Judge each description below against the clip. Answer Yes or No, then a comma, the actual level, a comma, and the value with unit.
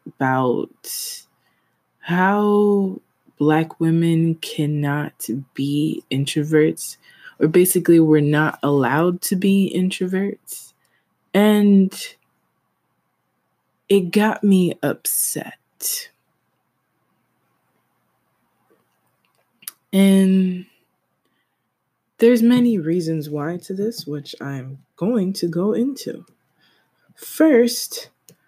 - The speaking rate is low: Yes, slow, 70 wpm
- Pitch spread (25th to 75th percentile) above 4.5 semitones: Yes, wide, 5.5 semitones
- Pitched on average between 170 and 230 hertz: Yes, medium, 185 Hz